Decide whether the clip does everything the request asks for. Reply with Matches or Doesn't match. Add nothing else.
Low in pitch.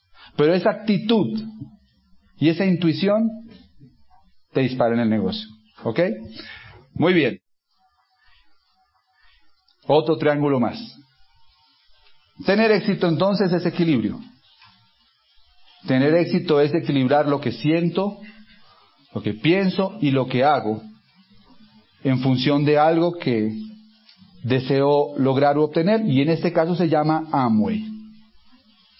Doesn't match